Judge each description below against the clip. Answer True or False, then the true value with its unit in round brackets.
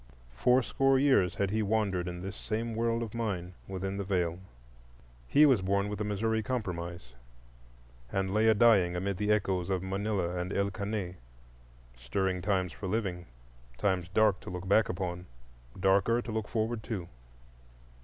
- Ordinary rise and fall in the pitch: True (3.2 semitones)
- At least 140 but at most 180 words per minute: True (160 wpm)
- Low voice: True (100 Hz)